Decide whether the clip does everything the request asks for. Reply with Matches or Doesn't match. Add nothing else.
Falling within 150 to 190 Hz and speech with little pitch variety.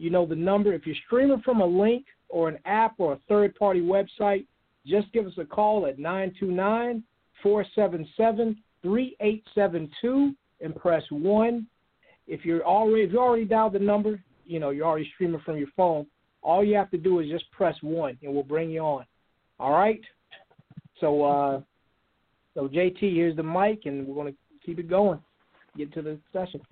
Doesn't match